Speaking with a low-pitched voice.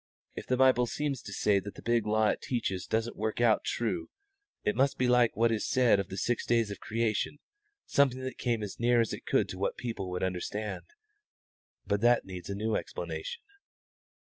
Yes: low, 115 Hz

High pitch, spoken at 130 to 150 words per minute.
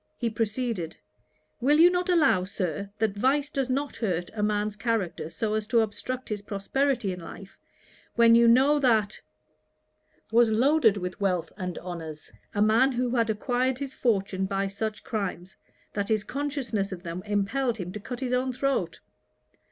No: high, 220 Hz; average, 165 wpm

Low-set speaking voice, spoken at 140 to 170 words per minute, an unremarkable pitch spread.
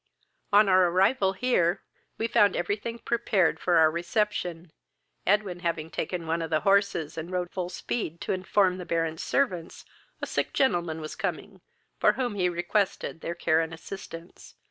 No: medium, 180 Hz; average, 165 wpm; average, 3.3 semitones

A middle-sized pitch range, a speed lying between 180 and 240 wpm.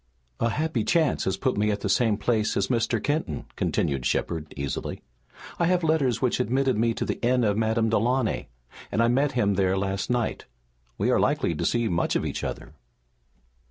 Yes: average, 4.1 semitones; average, 195 wpm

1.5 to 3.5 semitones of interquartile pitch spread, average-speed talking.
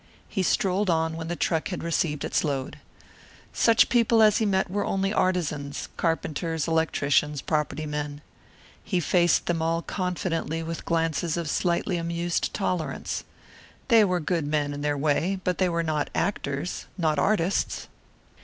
Yes: average, 3.1 semitones; average, 155 wpm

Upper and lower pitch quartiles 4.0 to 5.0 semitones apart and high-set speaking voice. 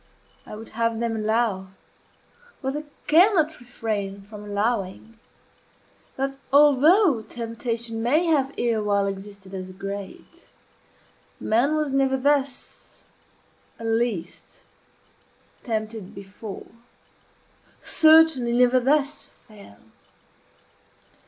Yes: average, 4.7 semitones; high, 230 Hz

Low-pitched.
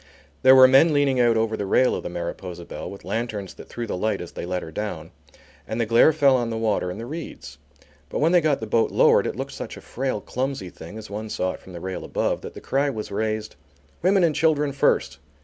Yes: low, 115 Hz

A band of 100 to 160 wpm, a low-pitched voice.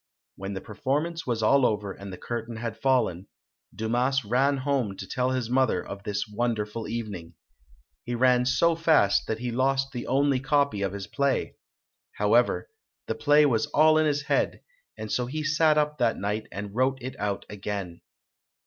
No: average, 175 wpm; low, 120 Hz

